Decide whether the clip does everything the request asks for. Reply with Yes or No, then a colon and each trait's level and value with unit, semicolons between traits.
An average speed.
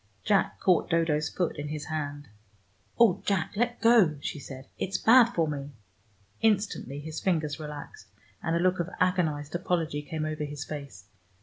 Yes: average, 165 wpm